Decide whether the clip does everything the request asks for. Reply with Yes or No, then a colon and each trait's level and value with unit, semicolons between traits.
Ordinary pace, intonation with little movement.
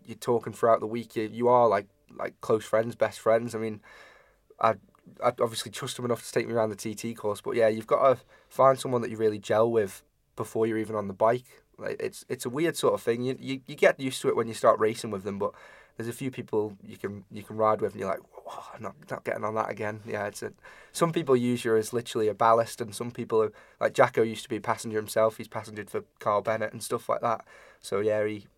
No: fast, 260 wpm; narrow, 2.1 semitones